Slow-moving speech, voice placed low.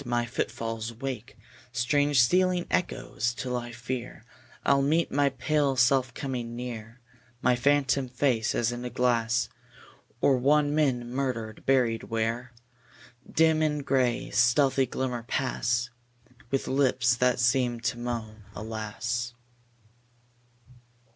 Yes: slow, 120 wpm; low, 125 Hz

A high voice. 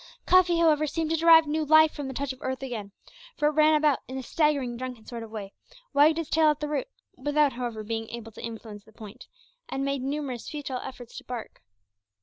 Yes: very high, 275 Hz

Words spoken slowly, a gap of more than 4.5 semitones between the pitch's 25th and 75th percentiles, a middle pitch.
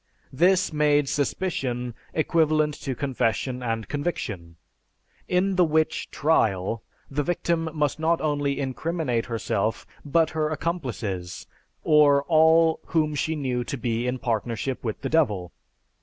Yes: slow, 125 wpm; average, 5.0 semitones; medium, 145 Hz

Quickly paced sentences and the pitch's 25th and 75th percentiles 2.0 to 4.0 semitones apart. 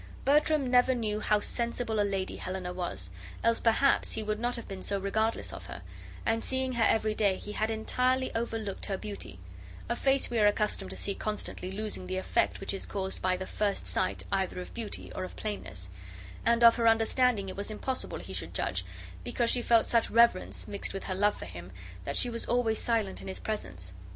Yes: fast, 210 wpm; average, 3.5 semitones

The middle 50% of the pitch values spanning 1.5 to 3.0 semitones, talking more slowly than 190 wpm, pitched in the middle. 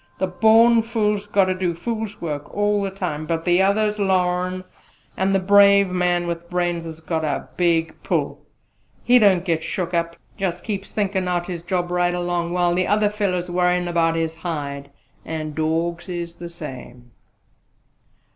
Yes: average, 2.7 semitones; average, 175 wpm; medium, 180 Hz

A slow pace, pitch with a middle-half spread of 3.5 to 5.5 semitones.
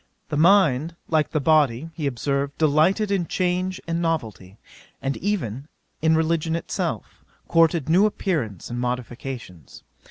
Yes: slow, 130 wpm; average, 4.6 semitones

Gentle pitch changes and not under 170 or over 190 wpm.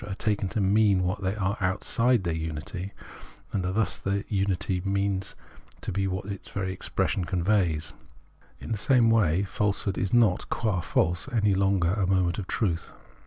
Yes: narrow, 2.2 semitones; average, 180 wpm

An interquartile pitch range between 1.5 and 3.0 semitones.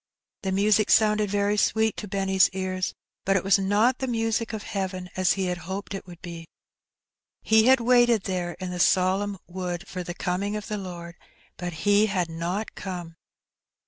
Yes: narrow, 2.6 semitones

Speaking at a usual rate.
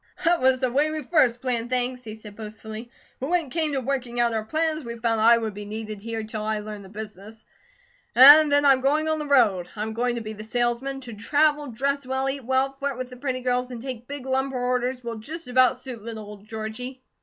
No: fast, 240 wpm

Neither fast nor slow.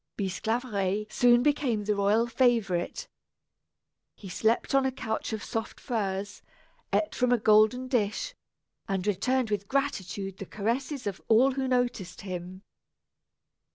No: slow, 130 wpm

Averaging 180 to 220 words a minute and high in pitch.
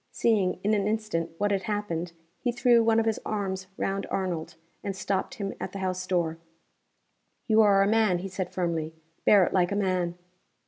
Yes: average, 190 wpm; high, 195 Hz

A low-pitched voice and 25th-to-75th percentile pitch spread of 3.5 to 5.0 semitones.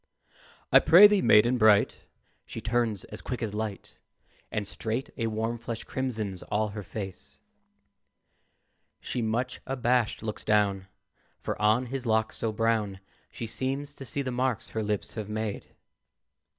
No: low, 110 Hz; average, 2.9 semitones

